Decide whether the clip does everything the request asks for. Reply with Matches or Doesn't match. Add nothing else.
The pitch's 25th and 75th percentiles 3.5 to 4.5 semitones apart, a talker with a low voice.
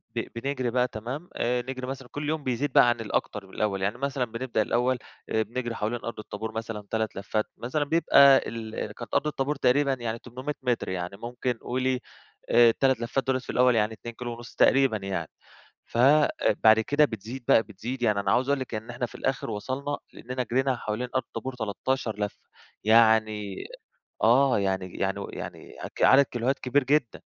Doesn't match